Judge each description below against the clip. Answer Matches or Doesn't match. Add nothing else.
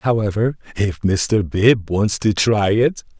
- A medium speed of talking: Matches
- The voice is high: Doesn't match